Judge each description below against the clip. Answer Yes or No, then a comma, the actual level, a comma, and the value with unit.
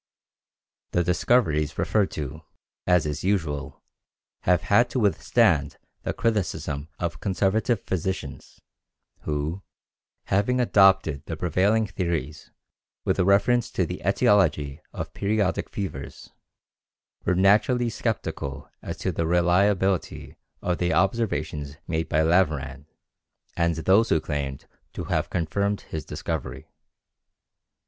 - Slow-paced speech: Yes, slow, 110 wpm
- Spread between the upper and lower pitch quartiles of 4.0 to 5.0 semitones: Yes, average, 4.7 semitones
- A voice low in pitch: Yes, very low, 90 Hz